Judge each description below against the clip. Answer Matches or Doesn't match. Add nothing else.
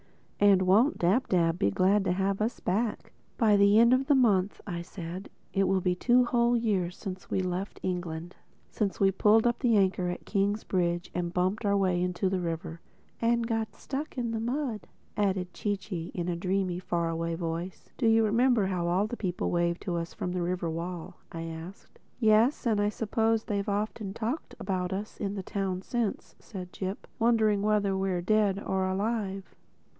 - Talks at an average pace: Matches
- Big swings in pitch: Doesn't match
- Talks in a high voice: Matches